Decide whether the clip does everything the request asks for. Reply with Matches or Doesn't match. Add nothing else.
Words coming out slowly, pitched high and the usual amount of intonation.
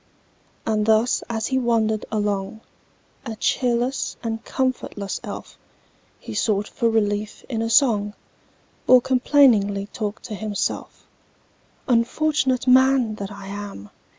Matches